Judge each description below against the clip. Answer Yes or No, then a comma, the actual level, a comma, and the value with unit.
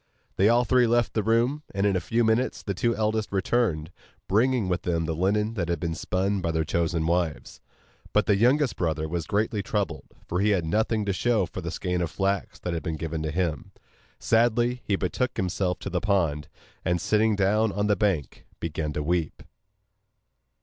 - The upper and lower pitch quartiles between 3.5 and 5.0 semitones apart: Yes, average, 4.5 semitones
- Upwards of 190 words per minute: Yes, average, 200 wpm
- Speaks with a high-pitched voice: No, very low, 95 Hz